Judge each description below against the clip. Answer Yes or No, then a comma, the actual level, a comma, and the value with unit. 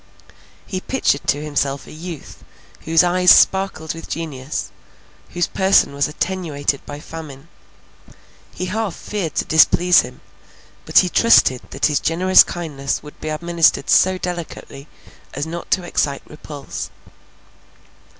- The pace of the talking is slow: Yes, slow, 130 wpm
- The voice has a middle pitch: Yes, medium, 160 Hz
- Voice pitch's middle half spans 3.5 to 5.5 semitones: Yes, average, 3.8 semitones